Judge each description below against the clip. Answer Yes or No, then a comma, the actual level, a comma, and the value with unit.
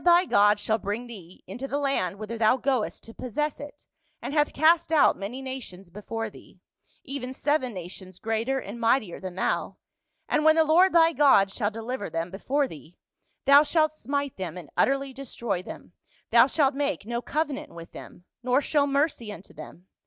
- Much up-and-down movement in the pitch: Yes, wide, 5.9 semitones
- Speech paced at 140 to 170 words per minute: No, average, 190 wpm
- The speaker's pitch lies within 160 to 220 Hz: No, very high, 250 Hz